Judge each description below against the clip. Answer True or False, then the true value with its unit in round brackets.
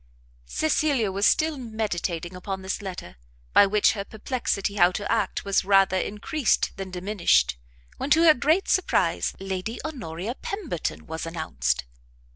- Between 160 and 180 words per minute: False (140 wpm)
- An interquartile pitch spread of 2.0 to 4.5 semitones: False (5.0 semitones)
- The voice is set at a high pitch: True (200 Hz)